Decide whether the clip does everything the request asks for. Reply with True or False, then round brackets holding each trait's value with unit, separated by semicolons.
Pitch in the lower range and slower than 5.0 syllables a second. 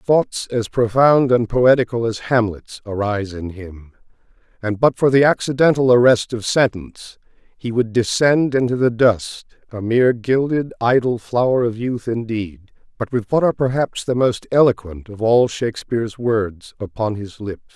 True (115 Hz; 4.7 syllables/s)